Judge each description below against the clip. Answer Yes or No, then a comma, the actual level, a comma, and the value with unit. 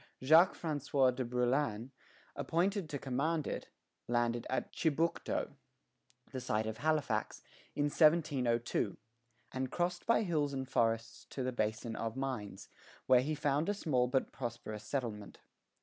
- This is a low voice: Yes, low, 130 Hz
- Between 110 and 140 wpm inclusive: Yes, slow, 135 wpm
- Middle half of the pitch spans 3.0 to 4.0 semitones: No, average, 4.5 semitones